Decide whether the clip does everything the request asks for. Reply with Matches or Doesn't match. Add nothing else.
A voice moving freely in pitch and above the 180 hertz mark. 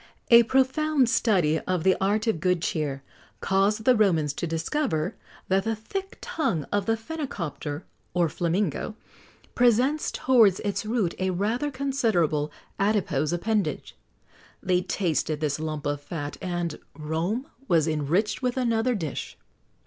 Matches